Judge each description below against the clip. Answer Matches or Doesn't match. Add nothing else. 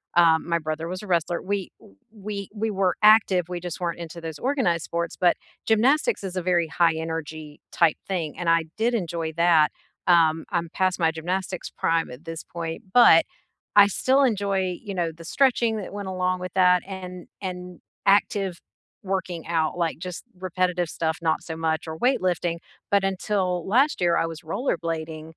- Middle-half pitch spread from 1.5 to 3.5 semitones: Matches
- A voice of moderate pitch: Matches